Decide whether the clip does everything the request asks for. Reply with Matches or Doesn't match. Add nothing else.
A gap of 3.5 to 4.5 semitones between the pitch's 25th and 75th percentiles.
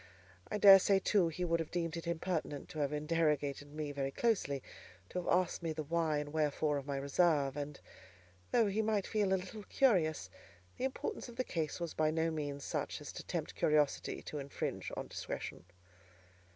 Matches